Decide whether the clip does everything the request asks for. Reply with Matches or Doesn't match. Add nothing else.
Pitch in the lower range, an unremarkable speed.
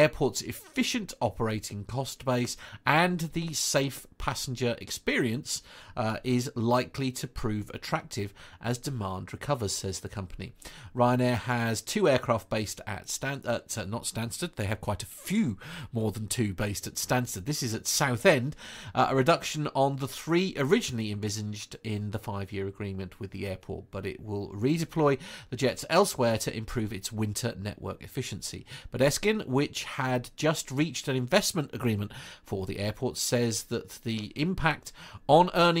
Matches